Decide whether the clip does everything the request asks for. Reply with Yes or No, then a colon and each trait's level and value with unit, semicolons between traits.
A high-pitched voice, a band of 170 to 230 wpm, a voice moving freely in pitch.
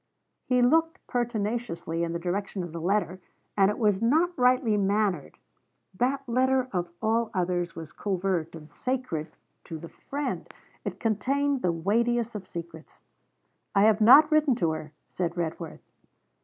No: high, 205 Hz; average, 150 wpm; wide, 6.3 semitones